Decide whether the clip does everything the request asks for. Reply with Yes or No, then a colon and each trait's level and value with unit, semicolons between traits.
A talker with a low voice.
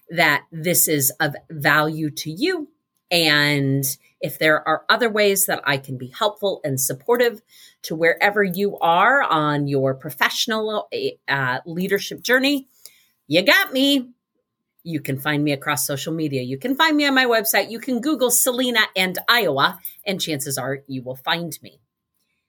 No: medium, 170 Hz